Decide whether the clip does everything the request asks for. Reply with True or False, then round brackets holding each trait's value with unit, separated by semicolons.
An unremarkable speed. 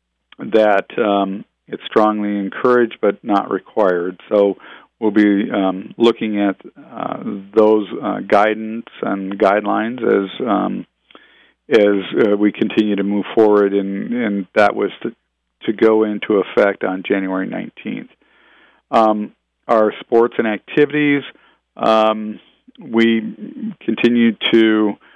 False (120 wpm)